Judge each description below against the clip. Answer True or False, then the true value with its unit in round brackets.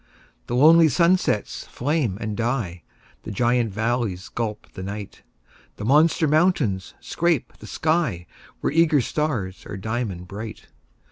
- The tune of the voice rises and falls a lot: True (7.1 semitones)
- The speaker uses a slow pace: True (130 wpm)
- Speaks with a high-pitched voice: False (120 Hz)